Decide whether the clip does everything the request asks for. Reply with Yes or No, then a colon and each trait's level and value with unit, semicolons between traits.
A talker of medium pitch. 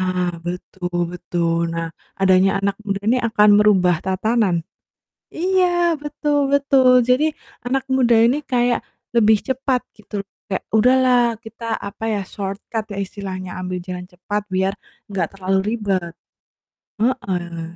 No: high, 205 Hz